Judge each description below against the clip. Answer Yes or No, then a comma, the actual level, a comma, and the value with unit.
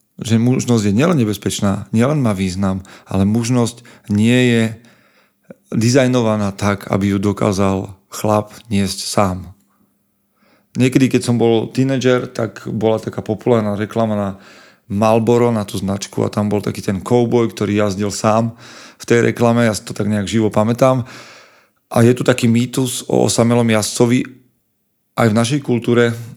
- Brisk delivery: No, average, 150 wpm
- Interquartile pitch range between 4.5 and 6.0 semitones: No, narrow, 2.6 semitones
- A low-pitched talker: Yes, low, 115 Hz